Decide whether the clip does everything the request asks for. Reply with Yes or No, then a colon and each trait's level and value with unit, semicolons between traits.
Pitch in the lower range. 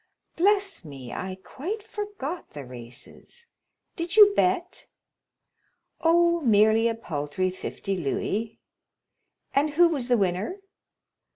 No: very high, 250 Hz